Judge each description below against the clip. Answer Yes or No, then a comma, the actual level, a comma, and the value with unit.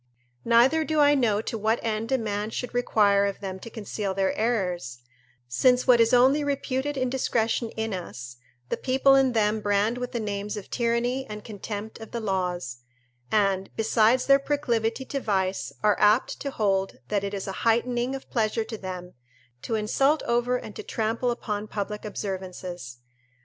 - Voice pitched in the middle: No, high, 220 Hz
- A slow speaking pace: No, average, 175 wpm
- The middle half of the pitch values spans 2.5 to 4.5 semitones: Yes, average, 3.6 semitones